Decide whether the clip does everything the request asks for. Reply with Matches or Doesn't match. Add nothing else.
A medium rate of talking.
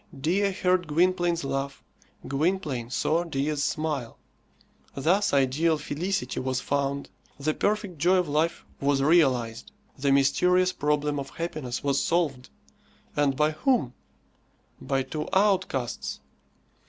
Doesn't match